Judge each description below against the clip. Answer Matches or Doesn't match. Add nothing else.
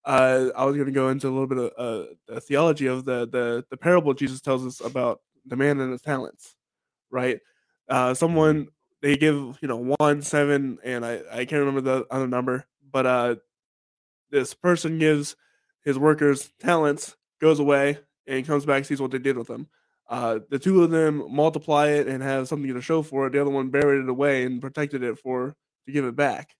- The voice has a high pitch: Doesn't match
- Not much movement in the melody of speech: Matches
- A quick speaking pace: Matches